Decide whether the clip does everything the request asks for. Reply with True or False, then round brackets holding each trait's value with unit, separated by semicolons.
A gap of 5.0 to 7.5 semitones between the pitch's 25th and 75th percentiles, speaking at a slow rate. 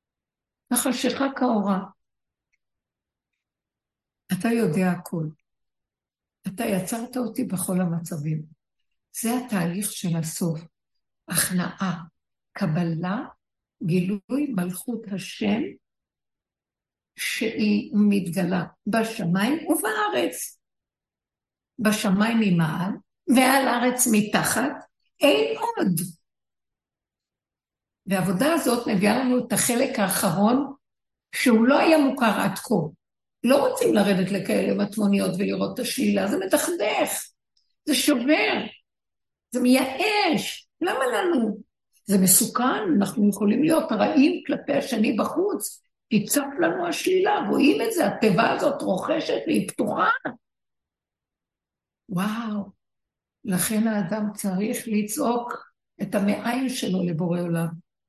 True (5.5 semitones; 95 wpm)